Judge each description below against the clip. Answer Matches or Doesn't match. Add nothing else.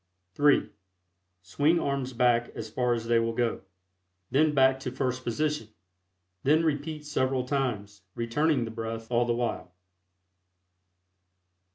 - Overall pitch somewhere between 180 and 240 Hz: Doesn't match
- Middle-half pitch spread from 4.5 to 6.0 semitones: Doesn't match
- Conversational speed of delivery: Doesn't match